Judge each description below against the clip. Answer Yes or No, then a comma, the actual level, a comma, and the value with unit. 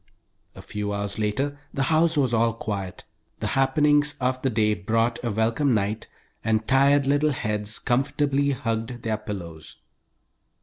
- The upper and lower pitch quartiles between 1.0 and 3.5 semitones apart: No, average, 4.6 semitones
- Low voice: Yes, low, 115 Hz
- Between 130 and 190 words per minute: Yes, average, 145 wpm